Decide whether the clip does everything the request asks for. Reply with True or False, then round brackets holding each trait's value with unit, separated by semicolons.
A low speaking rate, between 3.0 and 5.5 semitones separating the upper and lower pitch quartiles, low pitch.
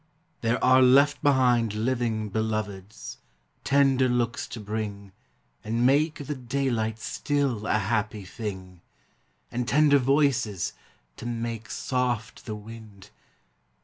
True (115 wpm; 3.4 semitones; 115 Hz)